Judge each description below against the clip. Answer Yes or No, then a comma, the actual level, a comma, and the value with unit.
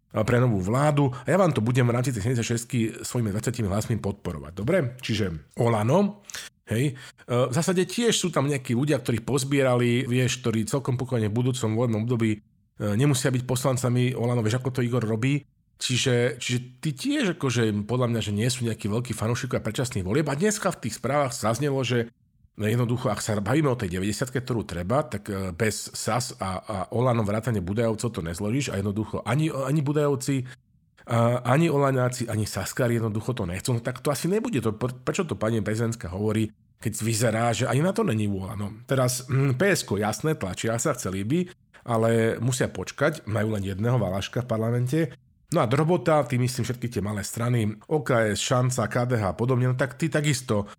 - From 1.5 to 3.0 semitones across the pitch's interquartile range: No, average, 3.8 semitones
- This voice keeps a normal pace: No, fast, 180 wpm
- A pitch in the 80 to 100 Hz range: No, low, 120 Hz